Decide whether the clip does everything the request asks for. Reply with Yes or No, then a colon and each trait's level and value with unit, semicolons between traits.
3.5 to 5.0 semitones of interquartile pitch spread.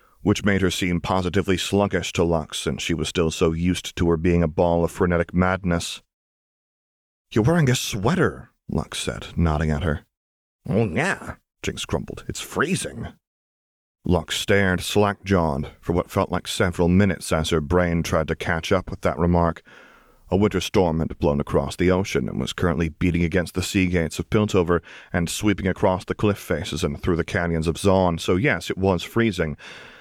No: narrow, 2.5 semitones